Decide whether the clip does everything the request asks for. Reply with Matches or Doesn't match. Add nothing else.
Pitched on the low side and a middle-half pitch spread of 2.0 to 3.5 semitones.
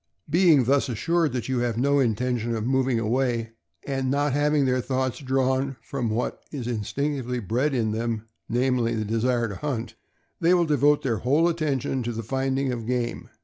Matches